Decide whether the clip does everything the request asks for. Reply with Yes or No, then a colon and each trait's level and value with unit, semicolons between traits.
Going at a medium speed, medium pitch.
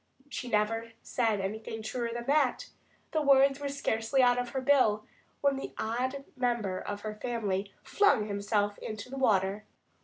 No: average, 160 wpm; high, 230 Hz